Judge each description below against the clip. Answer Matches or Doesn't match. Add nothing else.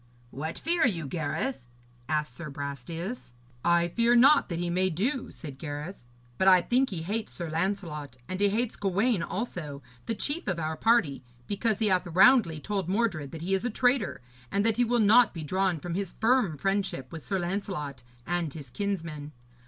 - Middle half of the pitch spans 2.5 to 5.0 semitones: Doesn't match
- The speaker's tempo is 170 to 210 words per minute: Matches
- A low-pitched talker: Doesn't match